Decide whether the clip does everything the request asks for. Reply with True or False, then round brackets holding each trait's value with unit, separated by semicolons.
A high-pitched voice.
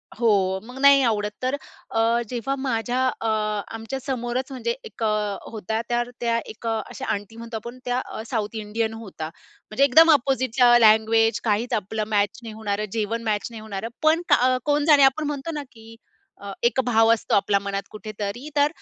True (230 Hz)